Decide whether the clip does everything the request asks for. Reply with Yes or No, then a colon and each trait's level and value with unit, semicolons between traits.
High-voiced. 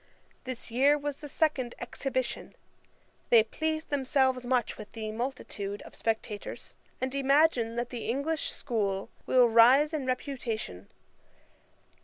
Yes: very high, 255 Hz